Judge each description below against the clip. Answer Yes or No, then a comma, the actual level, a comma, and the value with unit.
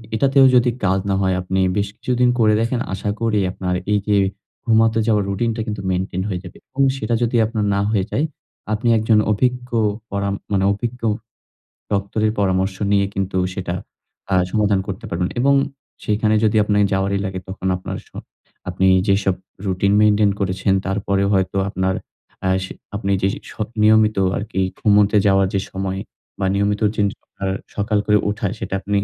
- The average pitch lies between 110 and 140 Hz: No, low, 100 Hz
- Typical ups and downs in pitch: No, narrow, 2.1 semitones